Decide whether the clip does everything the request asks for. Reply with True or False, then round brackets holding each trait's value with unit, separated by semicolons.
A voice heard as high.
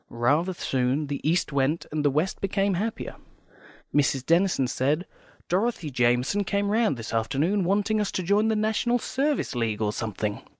False (165 Hz)